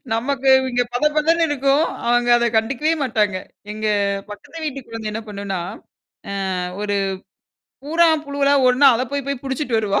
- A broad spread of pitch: No, average, 4.3 semitones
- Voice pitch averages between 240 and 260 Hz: Yes, very high, 255 Hz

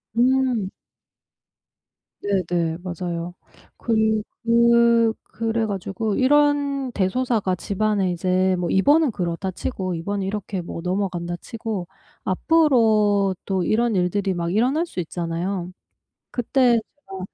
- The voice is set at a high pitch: Yes, high, 200 Hz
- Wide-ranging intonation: No, average, 4.4 semitones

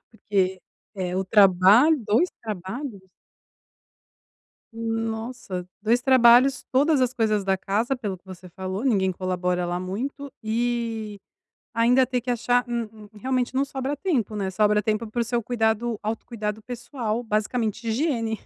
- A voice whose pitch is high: Yes, high, 225 Hz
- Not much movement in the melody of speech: No, average, 3.4 semitones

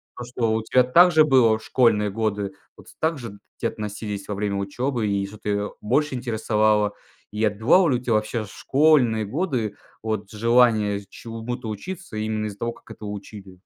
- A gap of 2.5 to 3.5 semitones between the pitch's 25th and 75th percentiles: Yes, average, 3.0 semitones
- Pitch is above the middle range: No, low, 110 Hz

